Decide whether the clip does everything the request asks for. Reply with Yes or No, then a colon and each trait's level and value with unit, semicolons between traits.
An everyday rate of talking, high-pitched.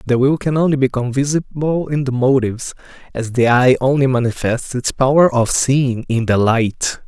No: average, 180 wpm; low, 130 Hz